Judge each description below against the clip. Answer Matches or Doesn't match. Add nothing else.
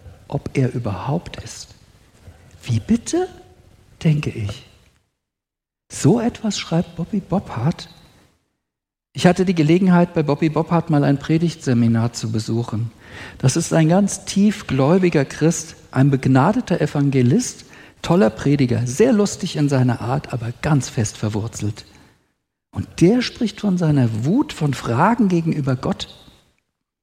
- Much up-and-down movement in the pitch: Matches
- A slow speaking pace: Matches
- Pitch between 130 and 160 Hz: Matches